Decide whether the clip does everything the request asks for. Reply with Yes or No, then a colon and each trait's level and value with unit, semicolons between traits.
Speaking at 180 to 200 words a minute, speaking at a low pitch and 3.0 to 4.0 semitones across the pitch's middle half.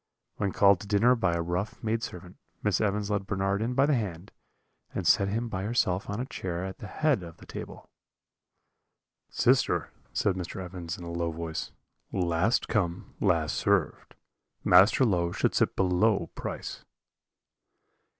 No: average, 160 wpm; very low, 95 Hz; average, 3.5 semitones